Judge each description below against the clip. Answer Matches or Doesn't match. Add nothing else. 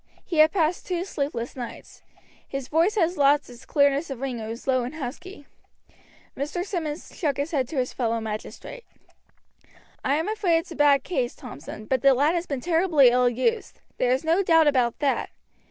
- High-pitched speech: Matches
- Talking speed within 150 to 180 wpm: Doesn't match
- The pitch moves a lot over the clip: Doesn't match